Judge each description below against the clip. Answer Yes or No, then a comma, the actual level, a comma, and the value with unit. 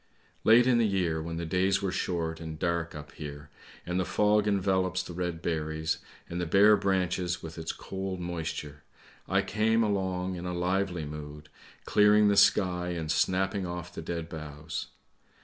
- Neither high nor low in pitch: No, very low, 90 Hz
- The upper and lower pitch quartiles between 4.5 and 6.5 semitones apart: No, average, 3.0 semitones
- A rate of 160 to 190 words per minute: Yes, average, 170 wpm